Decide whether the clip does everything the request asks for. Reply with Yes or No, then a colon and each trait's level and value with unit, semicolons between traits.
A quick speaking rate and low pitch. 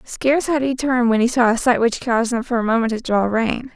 No: fast, 285 wpm; high, 240 Hz